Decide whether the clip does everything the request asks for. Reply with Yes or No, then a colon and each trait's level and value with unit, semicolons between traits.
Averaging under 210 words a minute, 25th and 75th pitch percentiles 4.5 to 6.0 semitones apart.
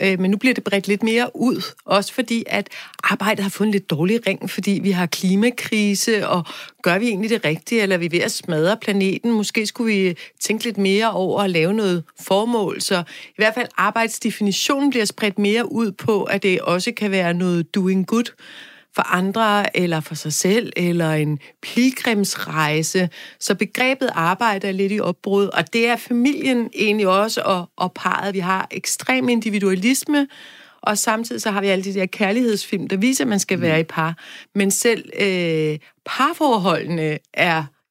No: average, 180 wpm; average, 3.6 semitones